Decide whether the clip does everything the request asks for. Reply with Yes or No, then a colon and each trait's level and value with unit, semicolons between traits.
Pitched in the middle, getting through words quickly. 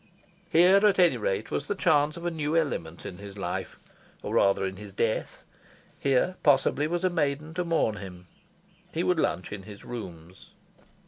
No: medium, 145 Hz; average, 180 wpm